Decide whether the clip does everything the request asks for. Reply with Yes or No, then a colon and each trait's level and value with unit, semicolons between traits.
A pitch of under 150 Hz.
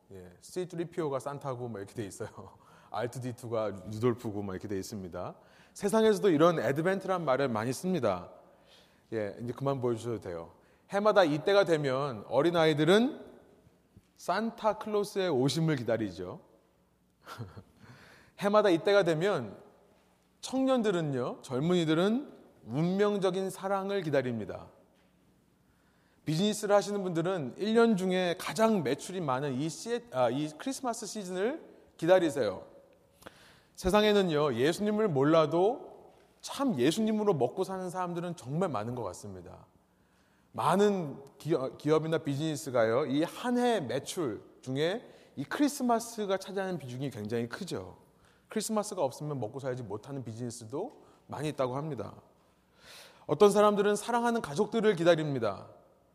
No: medium, 165 Hz